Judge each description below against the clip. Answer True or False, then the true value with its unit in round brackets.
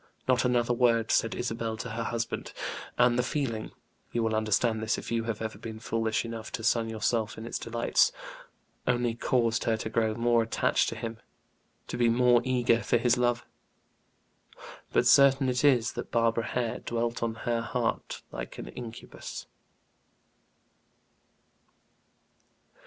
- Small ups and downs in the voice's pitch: True (1.3 semitones)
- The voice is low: True (115 Hz)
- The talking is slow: False (150 wpm)